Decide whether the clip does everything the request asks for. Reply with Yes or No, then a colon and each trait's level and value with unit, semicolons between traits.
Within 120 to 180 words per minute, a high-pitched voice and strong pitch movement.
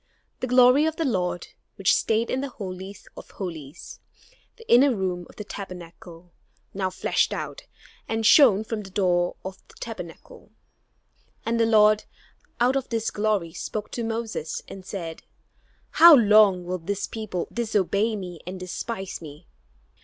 No: average, 155 wpm; high, 205 Hz; average, 4.1 semitones